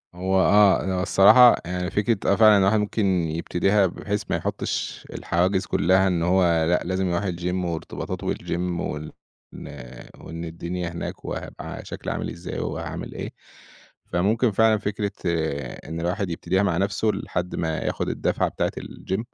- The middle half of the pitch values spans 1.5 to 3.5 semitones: Yes, average, 2.8 semitones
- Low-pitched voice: Yes, very low, 95 Hz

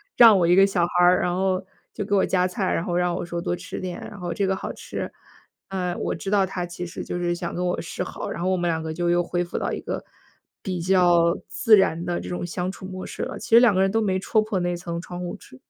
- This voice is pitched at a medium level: Yes, medium, 180 Hz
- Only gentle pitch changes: Yes, narrow, 1.7 semitones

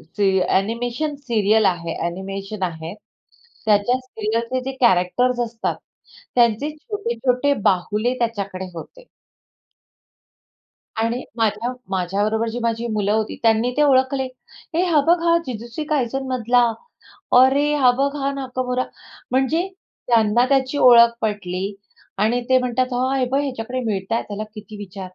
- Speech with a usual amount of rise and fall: Yes, average, 3.8 semitones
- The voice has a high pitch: Yes, high, 235 Hz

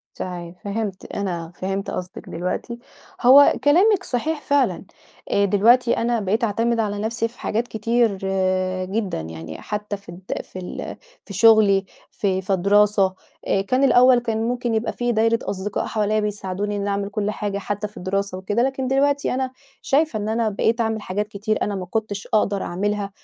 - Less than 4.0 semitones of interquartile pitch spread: Yes, average, 3.0 semitones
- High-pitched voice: Yes, high, 210 Hz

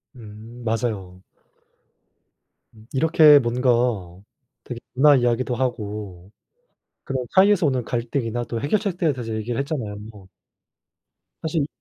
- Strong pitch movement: No, average, 4.2 semitones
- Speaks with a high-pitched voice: No, low, 120 Hz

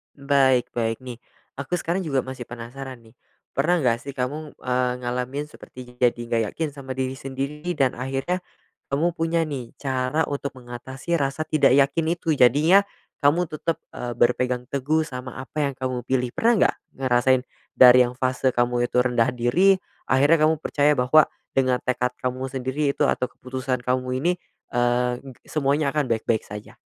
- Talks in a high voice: No, low, 130 Hz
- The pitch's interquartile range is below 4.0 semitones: Yes, average, 2.7 semitones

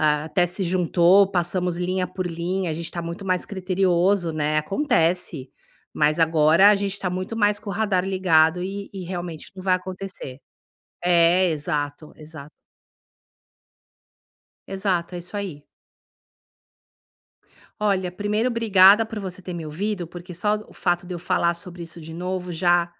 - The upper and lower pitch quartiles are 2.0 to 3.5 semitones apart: Yes, narrow, 2.4 semitones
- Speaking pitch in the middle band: Yes, medium, 180 Hz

